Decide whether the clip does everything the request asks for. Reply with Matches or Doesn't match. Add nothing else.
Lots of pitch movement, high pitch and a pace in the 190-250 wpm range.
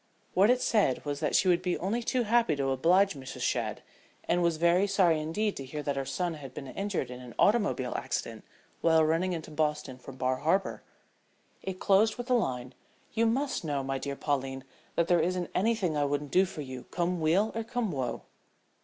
Doesn't match